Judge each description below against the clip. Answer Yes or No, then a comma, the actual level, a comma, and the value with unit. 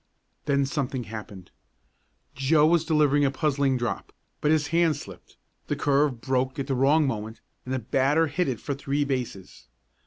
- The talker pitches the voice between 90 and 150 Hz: Yes, medium, 140 Hz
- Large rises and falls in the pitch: No, average, 2.7 semitones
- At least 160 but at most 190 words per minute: Yes, average, 165 wpm